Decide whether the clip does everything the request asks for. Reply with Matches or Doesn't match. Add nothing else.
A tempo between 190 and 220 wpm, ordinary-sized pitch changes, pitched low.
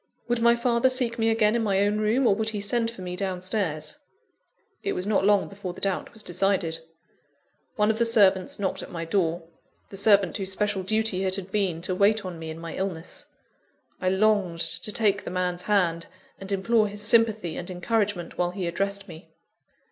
Doesn't match